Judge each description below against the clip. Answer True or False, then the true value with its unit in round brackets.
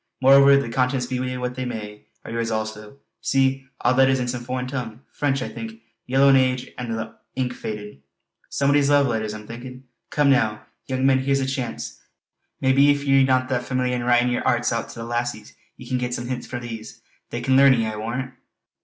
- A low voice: True (125 Hz)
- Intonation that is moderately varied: False (2.3 semitones)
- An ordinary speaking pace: False (215 wpm)